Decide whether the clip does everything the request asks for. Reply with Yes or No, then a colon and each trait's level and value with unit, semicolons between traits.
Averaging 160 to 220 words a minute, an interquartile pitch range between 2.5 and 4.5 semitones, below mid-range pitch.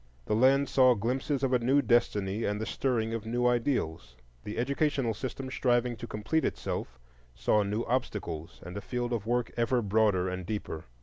Yes: average, 180 wpm; average, 3.5 semitones; low, 115 Hz